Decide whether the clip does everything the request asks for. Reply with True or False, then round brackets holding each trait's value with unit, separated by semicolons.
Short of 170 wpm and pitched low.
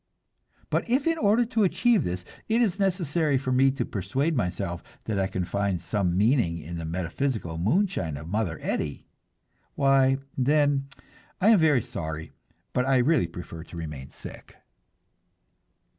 True (155 wpm; 125 Hz)